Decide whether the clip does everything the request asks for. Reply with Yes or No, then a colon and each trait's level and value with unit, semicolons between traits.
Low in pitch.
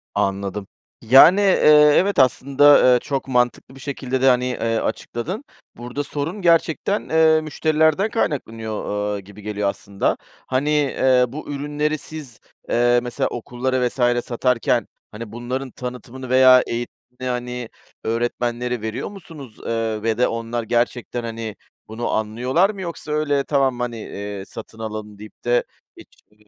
Yes: low, 125 Hz